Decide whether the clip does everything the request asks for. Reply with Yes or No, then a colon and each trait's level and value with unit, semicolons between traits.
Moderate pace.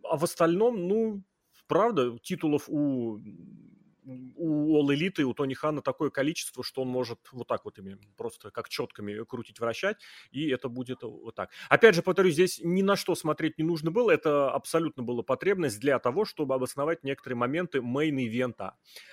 No: fast, 170 wpm